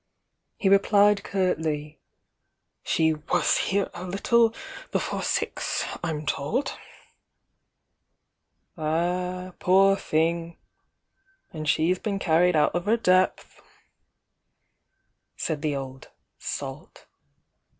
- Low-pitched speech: No, medium, 175 Hz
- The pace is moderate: No, slow, 95 wpm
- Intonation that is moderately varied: Yes, average, 3.9 semitones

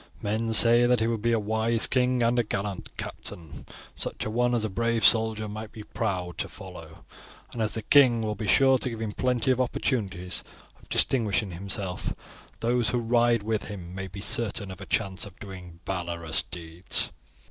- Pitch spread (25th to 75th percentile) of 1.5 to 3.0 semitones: No, average, 3.6 semitones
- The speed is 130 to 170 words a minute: No, average, 190 wpm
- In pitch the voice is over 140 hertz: No, low, 110 Hz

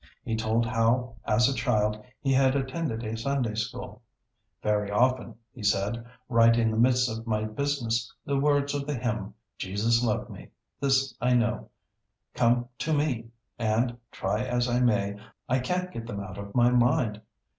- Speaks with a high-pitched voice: No, low, 120 Hz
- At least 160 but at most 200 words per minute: Yes, average, 170 wpm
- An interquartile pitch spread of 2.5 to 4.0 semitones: Yes, average, 2.8 semitones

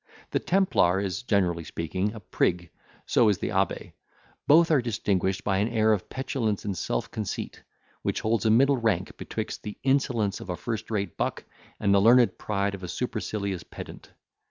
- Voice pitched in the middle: No, low, 105 Hz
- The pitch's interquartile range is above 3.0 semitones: Yes, average, 3.4 semitones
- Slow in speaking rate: No, average, 180 wpm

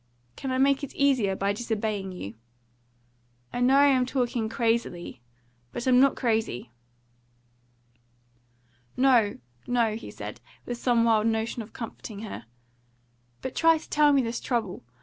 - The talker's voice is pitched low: No, high, 235 Hz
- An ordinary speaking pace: Yes, average, 145 wpm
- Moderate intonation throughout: Yes, average, 3.2 semitones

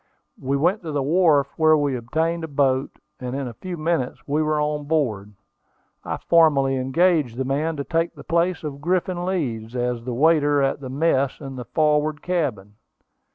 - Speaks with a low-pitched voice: No, medium, 145 Hz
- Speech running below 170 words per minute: No, average, 185 wpm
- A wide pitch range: No, average, 3.7 semitones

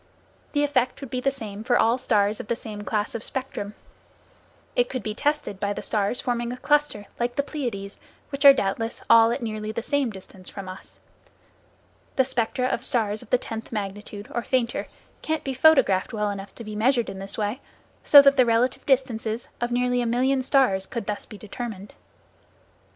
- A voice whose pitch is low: No, high, 235 Hz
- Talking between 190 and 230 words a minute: Yes, average, 195 wpm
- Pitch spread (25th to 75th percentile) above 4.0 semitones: No, average, 3.7 semitones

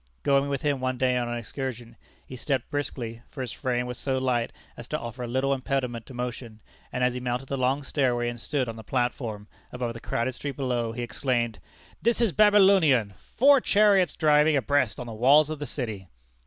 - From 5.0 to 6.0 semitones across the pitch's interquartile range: No, average, 3.0 semitones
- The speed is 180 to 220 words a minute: Yes, fast, 205 wpm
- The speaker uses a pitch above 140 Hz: No, low, 130 Hz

